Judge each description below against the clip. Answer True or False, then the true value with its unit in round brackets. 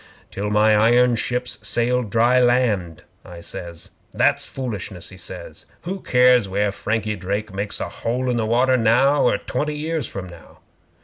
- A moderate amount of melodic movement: True (4.0 semitones)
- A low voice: True (115 Hz)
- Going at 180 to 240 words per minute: False (165 wpm)